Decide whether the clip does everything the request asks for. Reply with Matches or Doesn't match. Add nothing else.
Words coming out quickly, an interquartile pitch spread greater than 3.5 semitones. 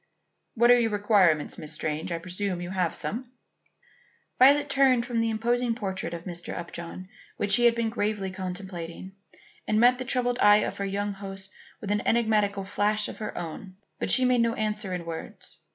Doesn't match